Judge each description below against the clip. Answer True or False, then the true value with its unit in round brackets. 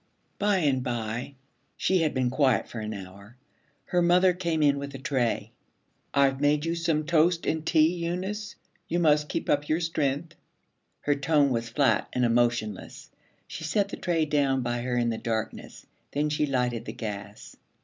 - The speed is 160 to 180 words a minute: True (175 wpm)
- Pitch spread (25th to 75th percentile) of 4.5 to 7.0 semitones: True (5.2 semitones)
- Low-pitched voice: False (145 Hz)